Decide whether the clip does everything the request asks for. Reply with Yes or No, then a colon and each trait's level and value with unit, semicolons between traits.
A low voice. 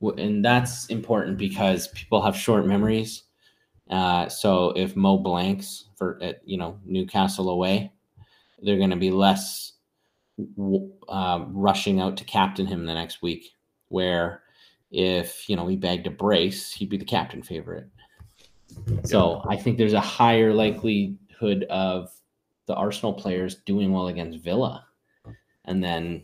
Yes: very low, 95 Hz